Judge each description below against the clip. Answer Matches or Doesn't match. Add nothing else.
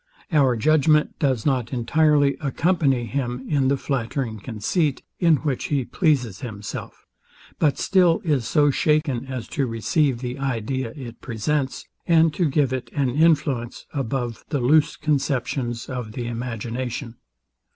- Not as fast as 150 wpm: Matches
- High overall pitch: Doesn't match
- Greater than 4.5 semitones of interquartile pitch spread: Doesn't match